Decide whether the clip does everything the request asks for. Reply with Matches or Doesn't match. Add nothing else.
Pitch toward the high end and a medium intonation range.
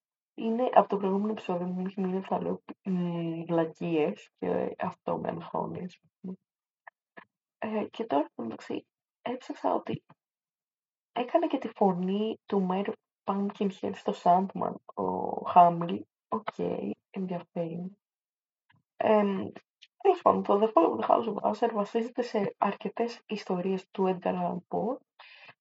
Matches